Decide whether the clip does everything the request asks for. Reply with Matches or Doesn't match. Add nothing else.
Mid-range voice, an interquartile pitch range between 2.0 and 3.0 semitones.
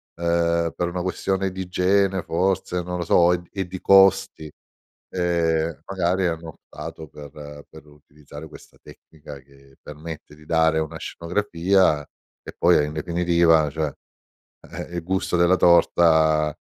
Doesn't match